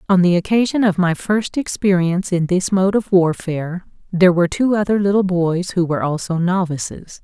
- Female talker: Yes, female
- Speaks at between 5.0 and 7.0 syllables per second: Yes, 5.5 syllables/s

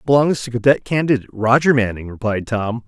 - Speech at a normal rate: Yes, average, 165 wpm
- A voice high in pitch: No, low, 120 Hz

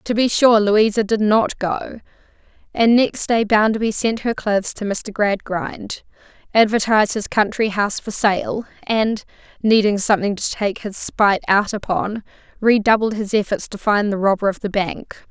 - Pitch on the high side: Yes, high, 210 Hz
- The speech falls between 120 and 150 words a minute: No, average, 165 wpm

